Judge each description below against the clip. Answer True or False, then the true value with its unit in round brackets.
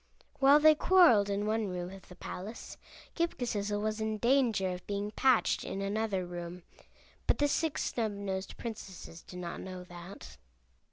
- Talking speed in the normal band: True (160 wpm)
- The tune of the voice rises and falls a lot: False (4.0 semitones)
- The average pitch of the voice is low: False (205 Hz)